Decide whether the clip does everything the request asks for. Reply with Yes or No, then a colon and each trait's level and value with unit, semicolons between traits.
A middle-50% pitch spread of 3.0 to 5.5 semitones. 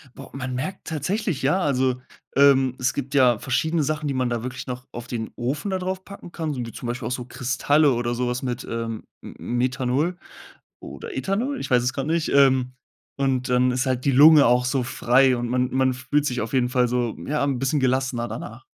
No: narrow, 2.6 semitones